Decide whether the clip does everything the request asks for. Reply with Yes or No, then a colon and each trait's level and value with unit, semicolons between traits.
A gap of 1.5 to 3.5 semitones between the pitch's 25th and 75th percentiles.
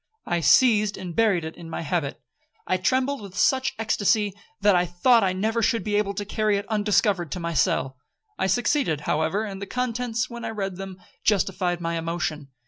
No: average, 4.1 semitones